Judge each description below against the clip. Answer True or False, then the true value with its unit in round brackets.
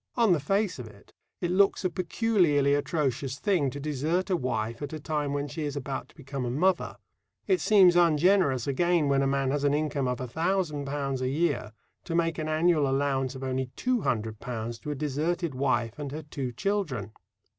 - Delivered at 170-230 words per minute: True (190 wpm)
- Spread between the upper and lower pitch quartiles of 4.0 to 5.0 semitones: True (4.5 semitones)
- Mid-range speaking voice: True (145 Hz)